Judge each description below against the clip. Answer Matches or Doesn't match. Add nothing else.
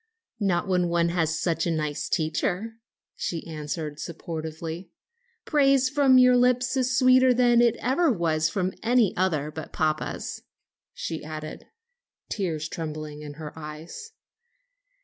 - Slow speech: Matches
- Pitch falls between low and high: Matches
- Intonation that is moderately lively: Doesn't match